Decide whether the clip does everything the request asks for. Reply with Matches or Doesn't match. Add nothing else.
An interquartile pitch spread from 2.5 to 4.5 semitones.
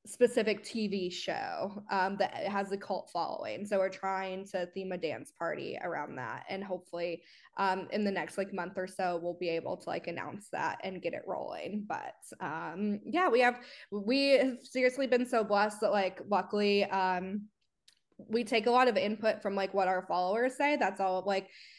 Matches